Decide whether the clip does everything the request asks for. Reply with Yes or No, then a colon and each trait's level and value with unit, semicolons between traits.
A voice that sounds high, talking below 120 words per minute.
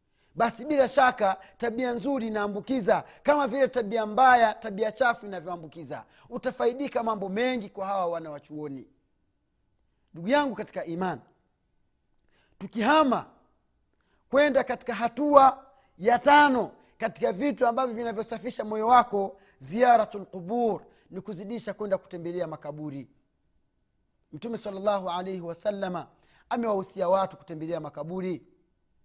Yes: high, 215 Hz; average, 105 wpm